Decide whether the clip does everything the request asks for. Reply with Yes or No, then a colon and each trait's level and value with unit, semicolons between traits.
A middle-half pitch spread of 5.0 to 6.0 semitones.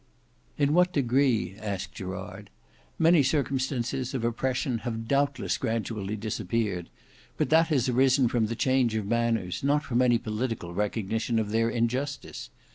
No: average, 3.5 semitones